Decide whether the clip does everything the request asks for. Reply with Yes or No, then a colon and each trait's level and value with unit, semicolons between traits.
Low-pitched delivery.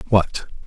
Yes: very low, 95 Hz